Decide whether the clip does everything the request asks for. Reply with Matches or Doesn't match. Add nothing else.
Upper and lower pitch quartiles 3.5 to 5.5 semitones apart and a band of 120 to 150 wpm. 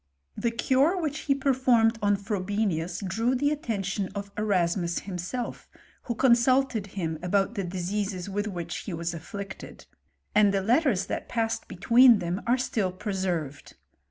Matches